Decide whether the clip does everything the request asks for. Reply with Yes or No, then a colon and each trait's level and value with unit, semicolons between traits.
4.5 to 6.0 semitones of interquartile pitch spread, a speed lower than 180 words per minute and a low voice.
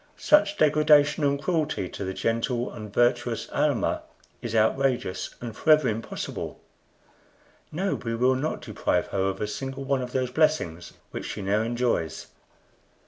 Yes: average, 5.2 semitones; average, 145 wpm; low, 125 Hz